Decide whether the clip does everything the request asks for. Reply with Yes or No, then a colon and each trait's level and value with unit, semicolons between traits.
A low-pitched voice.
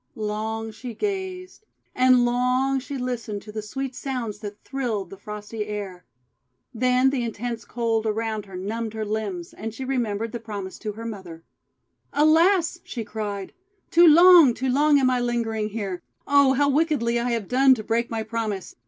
No: high, 230 Hz